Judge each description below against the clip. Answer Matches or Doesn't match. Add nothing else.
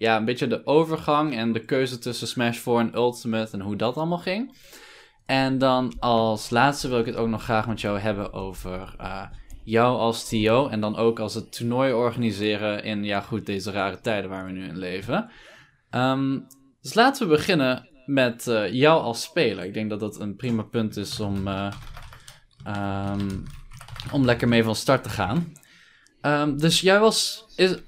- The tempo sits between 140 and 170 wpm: Doesn't match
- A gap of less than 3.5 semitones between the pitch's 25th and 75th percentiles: Doesn't match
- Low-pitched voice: Matches